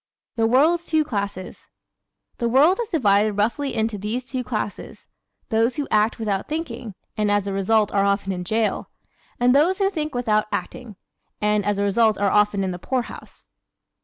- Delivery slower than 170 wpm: No, average, 180 wpm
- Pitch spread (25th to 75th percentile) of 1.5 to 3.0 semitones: No, average, 4.1 semitones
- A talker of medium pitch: No, high, 220 Hz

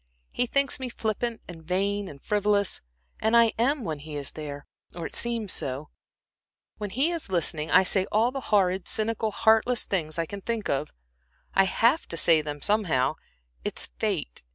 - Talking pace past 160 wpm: Yes, average, 180 wpm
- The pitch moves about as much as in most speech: No, wide, 6.0 semitones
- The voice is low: No, high, 200 Hz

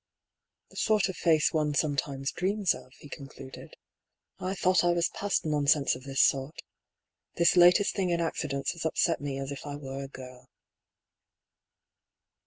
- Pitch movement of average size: Yes, average, 4.2 semitones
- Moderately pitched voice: Yes, medium, 150 Hz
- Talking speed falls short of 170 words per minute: No, average, 175 wpm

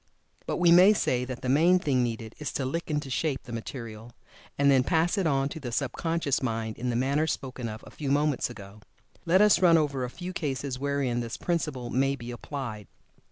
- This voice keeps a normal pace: No, fast, 215 wpm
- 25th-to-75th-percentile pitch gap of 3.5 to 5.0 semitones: Yes, average, 4.3 semitones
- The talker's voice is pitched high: No, low, 135 Hz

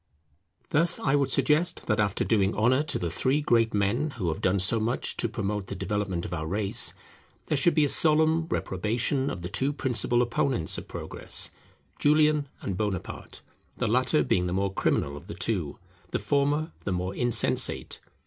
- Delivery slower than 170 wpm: No, average, 180 wpm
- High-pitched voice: No, low, 115 Hz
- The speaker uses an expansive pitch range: Yes, wide, 6.9 semitones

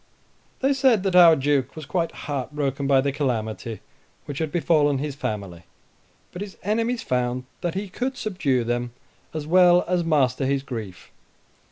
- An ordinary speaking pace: Yes, average, 165 wpm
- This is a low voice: No, medium, 145 Hz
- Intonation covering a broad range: Yes, wide, 5.8 semitones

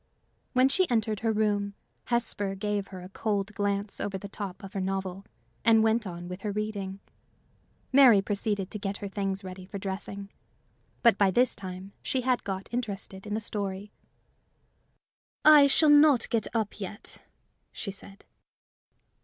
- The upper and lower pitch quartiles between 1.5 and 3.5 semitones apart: Yes, narrow, 2.4 semitones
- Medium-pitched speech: No, high, 205 Hz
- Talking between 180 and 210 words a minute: No, average, 160 wpm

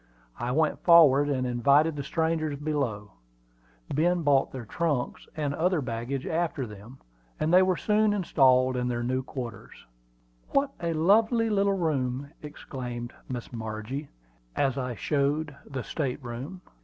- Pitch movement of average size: Yes, average, 4.5 semitones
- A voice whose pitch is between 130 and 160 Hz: Yes, medium, 140 Hz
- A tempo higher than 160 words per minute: No, average, 145 wpm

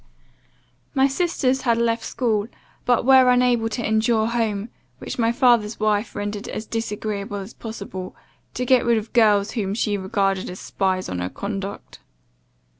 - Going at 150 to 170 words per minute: Yes, average, 155 wpm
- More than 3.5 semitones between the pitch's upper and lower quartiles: No, average, 2.8 semitones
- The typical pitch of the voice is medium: No, high, 220 Hz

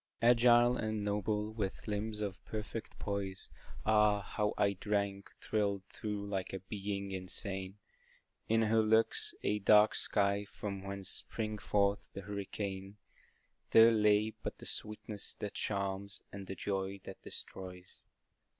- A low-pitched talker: Yes, low, 100 Hz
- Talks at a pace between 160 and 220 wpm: No, slow, 135 wpm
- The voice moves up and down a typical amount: No, narrow, 1.5 semitones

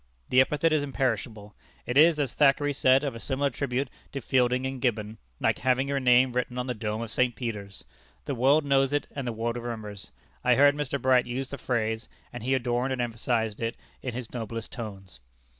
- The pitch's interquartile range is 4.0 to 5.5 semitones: No, average, 2.9 semitones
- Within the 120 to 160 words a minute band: No, fast, 205 wpm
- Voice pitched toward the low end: Yes, low, 125 Hz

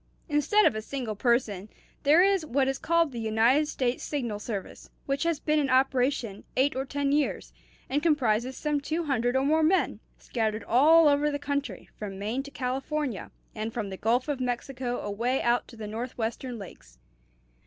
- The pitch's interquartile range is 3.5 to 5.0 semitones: Yes, average, 4.2 semitones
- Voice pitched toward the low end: No, very high, 260 Hz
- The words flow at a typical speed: Yes, average, 180 wpm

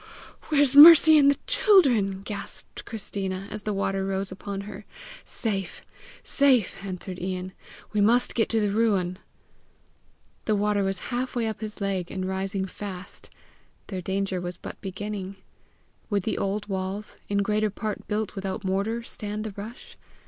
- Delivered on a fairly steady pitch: Yes, narrow, 2.3 semitones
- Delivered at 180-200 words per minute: No, average, 150 wpm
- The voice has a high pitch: Yes, high, 200 Hz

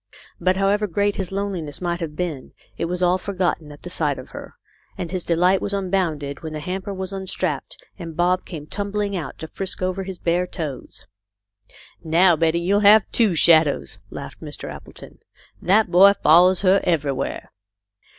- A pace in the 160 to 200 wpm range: Yes, average, 180 wpm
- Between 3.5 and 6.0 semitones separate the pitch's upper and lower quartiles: No, average, 3.1 semitones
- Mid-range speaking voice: Yes, medium, 180 Hz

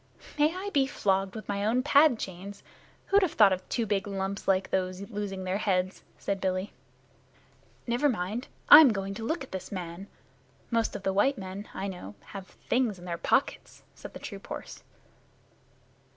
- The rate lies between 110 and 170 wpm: No, average, 180 wpm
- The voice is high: Yes, high, 200 Hz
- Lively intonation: No, average, 3.9 semitones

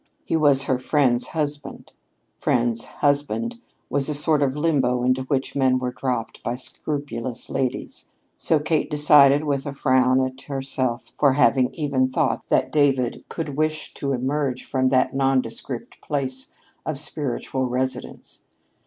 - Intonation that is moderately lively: No, narrow, 2.2 semitones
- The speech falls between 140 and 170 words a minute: Yes, average, 145 wpm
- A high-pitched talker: No, low, 135 Hz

